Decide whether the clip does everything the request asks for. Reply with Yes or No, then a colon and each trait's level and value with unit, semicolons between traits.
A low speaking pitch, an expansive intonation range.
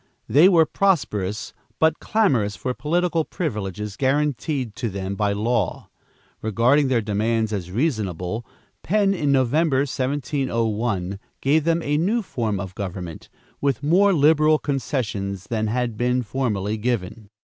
Yes: low, 120 Hz; wide, 6.1 semitones